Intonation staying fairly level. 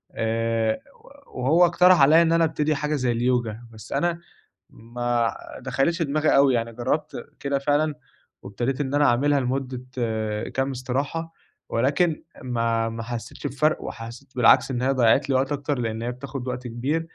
No: average, 3.6 semitones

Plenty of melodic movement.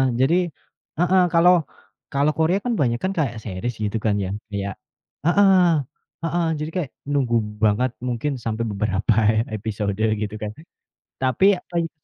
Yes: wide, 7.9 semitones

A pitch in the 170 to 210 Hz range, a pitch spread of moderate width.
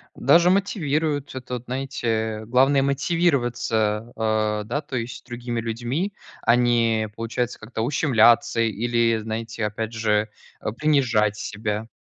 No: low, 120 Hz; average, 3.4 semitones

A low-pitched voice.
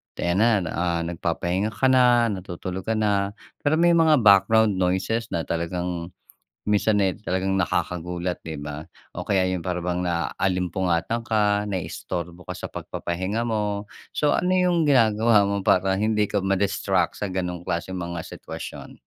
Yes: very low, 95 Hz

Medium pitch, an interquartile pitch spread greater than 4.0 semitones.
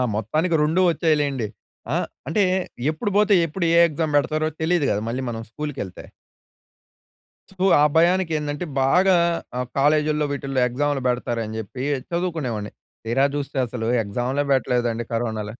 Yes: medium, 145 Hz; average, 5.0 semitones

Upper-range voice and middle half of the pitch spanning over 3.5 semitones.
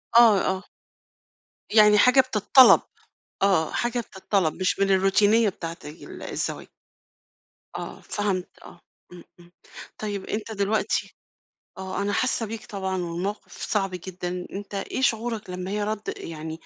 No: high, 200 Hz; average, 2.7 semitones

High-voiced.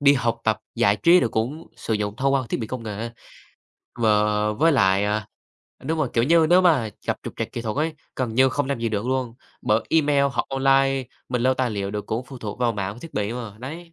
No: low, 125 Hz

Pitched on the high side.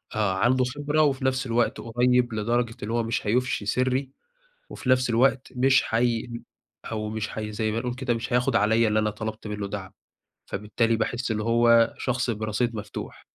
No: low, 115 Hz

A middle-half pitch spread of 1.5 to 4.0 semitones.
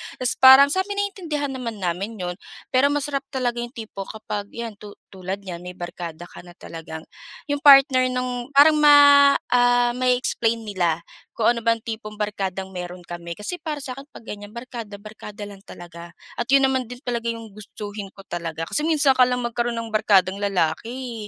No: average, 4.7 semitones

